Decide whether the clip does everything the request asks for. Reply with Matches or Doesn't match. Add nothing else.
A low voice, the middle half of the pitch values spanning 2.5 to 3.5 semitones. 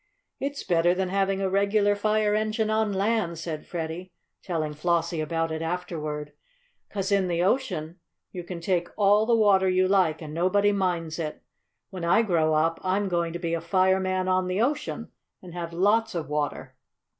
Doesn't match